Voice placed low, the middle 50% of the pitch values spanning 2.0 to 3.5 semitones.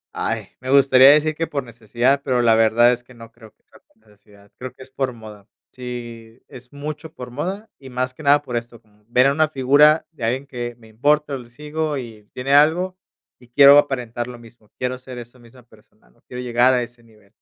Yes: low, 125 Hz; average, 3.1 semitones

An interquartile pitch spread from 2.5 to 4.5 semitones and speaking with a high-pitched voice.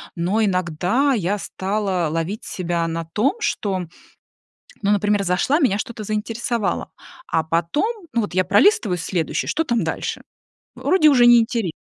No: average, 5.0 semitones; high, 205 Hz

